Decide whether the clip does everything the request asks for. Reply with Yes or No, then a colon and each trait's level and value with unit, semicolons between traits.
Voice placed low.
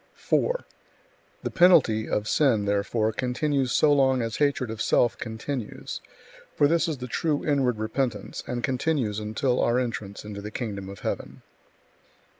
Yes: low, 120 Hz